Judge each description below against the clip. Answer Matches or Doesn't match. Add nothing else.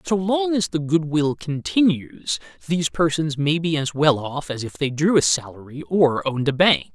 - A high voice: Doesn't match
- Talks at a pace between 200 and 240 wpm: Matches